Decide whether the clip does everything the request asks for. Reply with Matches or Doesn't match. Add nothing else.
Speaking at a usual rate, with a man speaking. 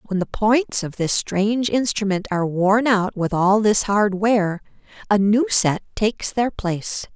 Doesn't match